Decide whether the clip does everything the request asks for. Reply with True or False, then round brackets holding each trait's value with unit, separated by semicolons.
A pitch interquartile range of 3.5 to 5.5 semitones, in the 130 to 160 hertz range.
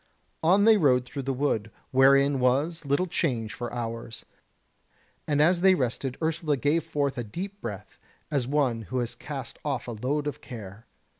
True (3.9 semitones; 140 Hz)